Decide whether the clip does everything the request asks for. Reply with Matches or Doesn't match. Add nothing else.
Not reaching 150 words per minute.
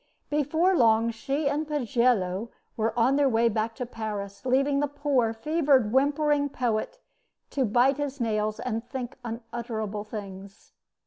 Matches